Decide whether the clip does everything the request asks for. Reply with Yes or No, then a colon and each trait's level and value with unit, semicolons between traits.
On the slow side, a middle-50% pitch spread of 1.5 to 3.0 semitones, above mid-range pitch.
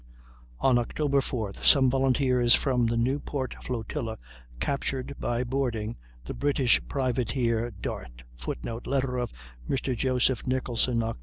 No: slow, 125 wpm; narrow, 2.4 semitones; low, 125 Hz